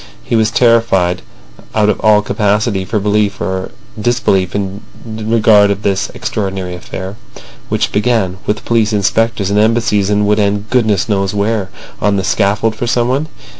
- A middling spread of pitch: No, narrow, 2.2 semitones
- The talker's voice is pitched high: No, low, 105 Hz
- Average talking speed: Yes, average, 150 wpm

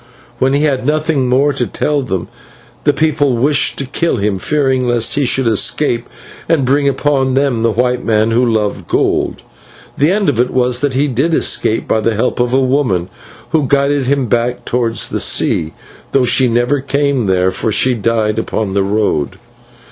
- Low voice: Yes, low, 125 Hz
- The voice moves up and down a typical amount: Yes, average, 3.6 semitones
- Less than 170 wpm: No, average, 185 wpm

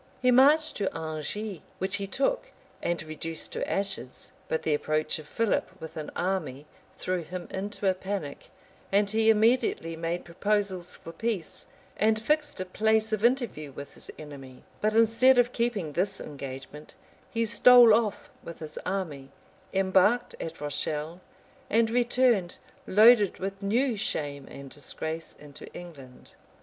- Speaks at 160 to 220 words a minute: No, average, 145 wpm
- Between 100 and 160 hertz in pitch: No, high, 190 Hz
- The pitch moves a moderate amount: No, wide, 6.0 semitones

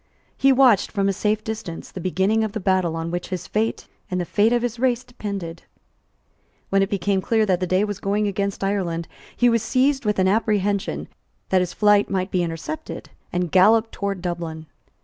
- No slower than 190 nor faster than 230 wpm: Yes, average, 195 wpm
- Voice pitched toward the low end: No, high, 200 Hz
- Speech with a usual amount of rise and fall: Yes, average, 3.1 semitones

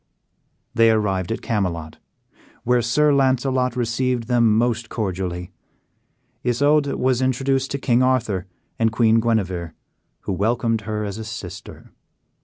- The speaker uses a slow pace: Yes, slow, 125 wpm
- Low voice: Yes, low, 115 Hz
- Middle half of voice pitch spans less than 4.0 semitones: Yes, average, 3.4 semitones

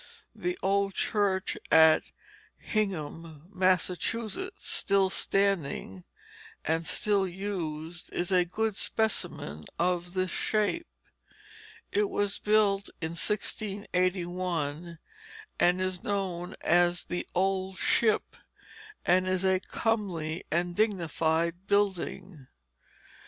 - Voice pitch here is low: No, medium, 185 Hz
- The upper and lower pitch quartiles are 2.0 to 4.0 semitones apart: Yes, average, 2.8 semitones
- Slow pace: Yes, slow, 95 wpm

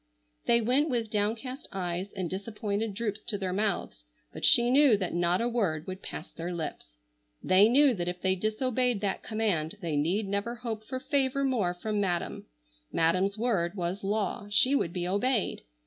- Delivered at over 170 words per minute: Yes, average, 180 wpm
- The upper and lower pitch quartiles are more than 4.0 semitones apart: Yes, average, 4.5 semitones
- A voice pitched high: Yes, high, 205 Hz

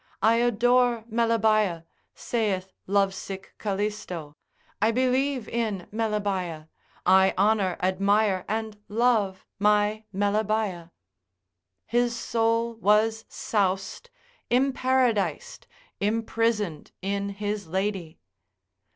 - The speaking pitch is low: No, high, 210 Hz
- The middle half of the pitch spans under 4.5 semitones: Yes, average, 2.9 semitones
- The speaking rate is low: Yes, slow, 80 wpm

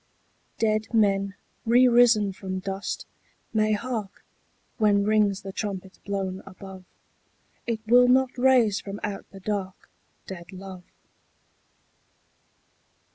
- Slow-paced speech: Yes, slow, 110 wpm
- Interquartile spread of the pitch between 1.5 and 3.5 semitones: Yes, narrow, 2.6 semitones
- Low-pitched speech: No, high, 205 Hz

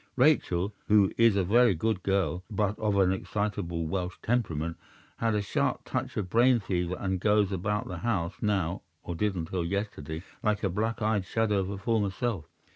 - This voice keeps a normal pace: Yes, average, 165 wpm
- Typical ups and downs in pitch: Yes, average, 3.2 semitones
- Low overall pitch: Yes, low, 100 Hz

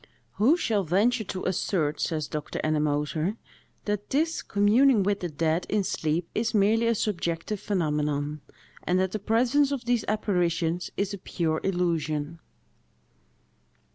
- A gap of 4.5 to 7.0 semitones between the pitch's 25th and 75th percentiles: Yes, average, 5.0 semitones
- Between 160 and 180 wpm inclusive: No, average, 140 wpm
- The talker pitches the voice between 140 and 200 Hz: Yes, medium, 185 Hz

